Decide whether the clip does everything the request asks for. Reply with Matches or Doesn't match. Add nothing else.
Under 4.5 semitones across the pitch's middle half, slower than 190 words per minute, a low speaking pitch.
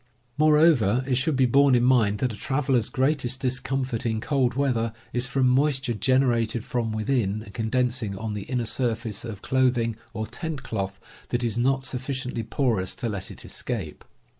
Matches